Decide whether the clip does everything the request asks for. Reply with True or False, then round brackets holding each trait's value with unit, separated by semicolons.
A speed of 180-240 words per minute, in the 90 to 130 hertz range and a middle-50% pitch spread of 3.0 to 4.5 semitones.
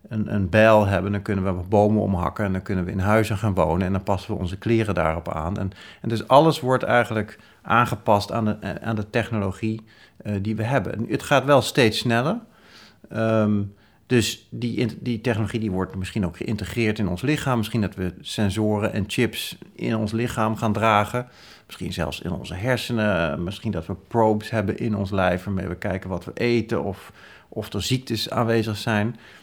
False (195 wpm; 110 Hz; 2.6 semitones)